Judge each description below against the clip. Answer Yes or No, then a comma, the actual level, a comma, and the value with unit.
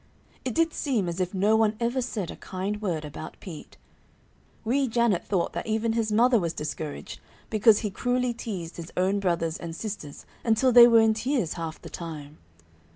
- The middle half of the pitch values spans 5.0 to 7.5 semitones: Yes, wide, 5.5 semitones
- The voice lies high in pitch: Yes, high, 210 Hz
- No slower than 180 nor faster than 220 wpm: Yes, average, 185 wpm